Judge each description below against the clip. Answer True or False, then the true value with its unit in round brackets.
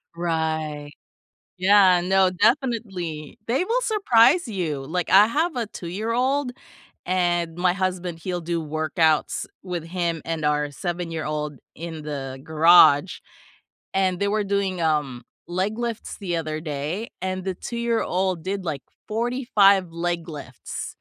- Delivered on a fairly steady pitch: False (4.2 semitones)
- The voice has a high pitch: False (180 Hz)